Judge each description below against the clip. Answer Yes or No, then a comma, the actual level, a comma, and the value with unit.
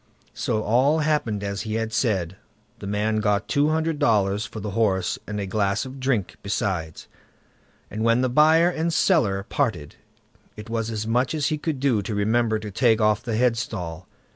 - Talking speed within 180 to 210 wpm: Yes, average, 185 wpm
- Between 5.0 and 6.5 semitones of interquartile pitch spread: No, average, 4.1 semitones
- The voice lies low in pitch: Yes, low, 110 Hz